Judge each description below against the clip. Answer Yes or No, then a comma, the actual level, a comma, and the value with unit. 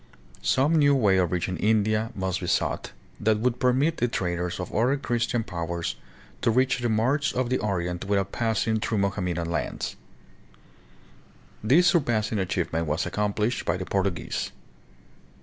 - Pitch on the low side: Yes, low, 105 Hz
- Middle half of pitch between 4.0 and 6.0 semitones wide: Yes, average, 5.0 semitones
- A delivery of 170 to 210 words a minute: No, average, 150 wpm